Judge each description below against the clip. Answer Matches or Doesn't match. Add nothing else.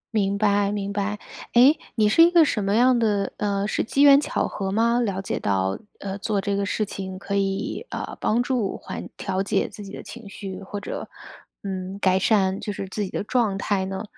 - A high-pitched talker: Matches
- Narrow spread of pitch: Matches